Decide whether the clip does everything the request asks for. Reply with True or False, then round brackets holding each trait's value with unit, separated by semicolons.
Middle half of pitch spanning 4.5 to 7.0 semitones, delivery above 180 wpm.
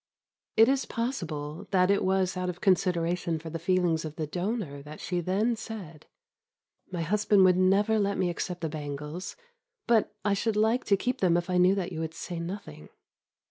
False (3.5 semitones; 190 wpm)